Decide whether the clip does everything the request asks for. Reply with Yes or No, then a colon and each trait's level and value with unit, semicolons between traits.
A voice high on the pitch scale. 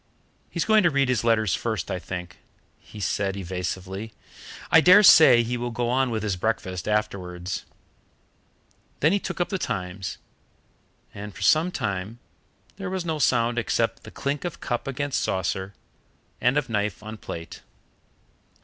No: low, 115 Hz